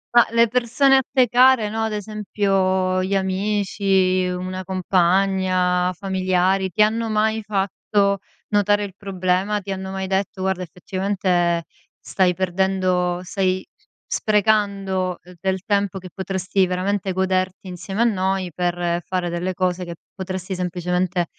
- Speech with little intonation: Yes, narrow, 1.7 semitones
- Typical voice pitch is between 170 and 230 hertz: Yes, high, 190 Hz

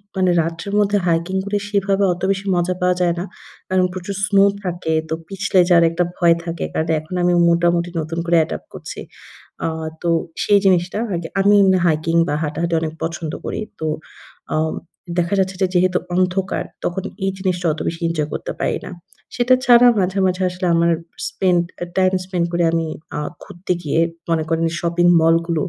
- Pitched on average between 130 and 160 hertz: No, medium, 175 Hz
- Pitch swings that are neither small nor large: No, narrow, 2.2 semitones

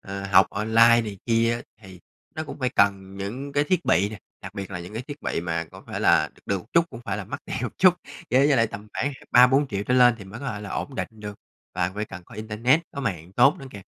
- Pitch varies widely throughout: No, average, 4.5 semitones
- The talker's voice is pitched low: Yes, low, 110 Hz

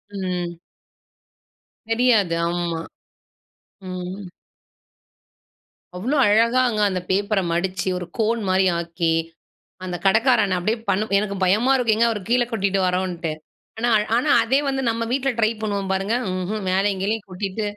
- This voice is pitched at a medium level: No, high, 200 Hz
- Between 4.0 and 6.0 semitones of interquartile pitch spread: No, average, 3.6 semitones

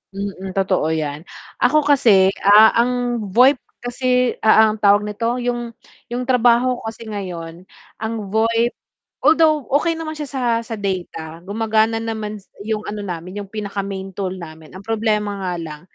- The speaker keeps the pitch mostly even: No, average, 4.0 semitones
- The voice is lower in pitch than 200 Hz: No, high, 220 Hz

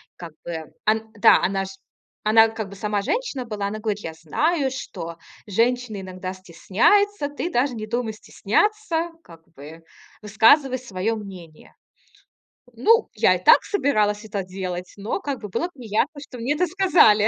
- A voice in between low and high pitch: No, high, 220 Hz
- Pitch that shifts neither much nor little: No, wide, 6.5 semitones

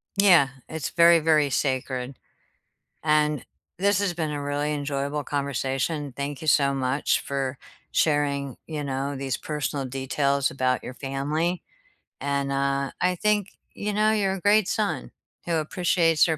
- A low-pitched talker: No, medium, 145 Hz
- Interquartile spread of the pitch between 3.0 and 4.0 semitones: Yes, average, 3.4 semitones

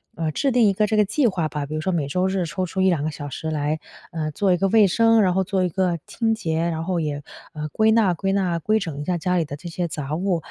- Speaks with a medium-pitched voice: Yes, medium, 180 Hz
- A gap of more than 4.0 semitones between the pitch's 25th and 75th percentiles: No, average, 3.7 semitones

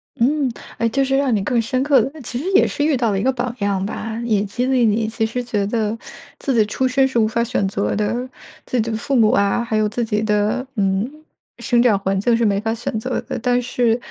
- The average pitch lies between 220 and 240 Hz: Yes, high, 230 Hz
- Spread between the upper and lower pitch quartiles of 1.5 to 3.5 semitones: Yes, average, 3.1 semitones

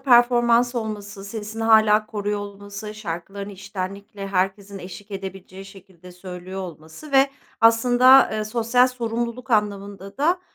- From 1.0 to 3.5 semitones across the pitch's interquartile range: Yes, average, 3.2 semitones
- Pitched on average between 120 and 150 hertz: No, high, 205 Hz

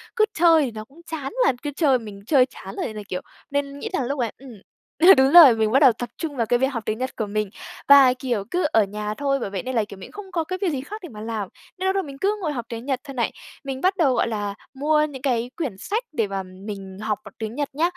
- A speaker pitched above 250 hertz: Yes, very high, 260 Hz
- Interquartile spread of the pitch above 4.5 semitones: Yes, wide, 5.4 semitones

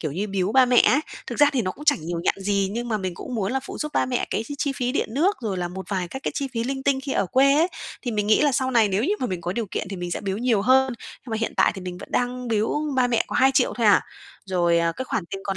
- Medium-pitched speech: No, high, 230 Hz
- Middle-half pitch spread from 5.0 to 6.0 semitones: Yes, wide, 5.4 semitones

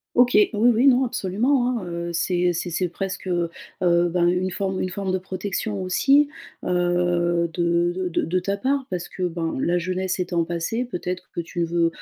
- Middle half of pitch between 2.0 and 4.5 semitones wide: Yes, narrow, 2.4 semitones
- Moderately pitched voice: Yes, medium, 180 Hz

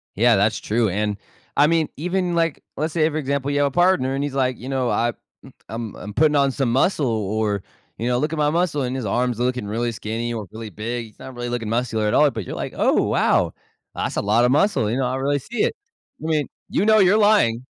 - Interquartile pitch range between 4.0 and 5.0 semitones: Yes, average, 4.7 semitones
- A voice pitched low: Yes, low, 125 Hz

